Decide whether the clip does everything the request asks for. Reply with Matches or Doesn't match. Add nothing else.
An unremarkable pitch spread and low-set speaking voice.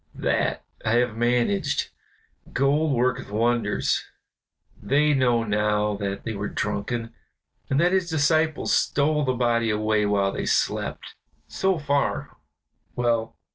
Matches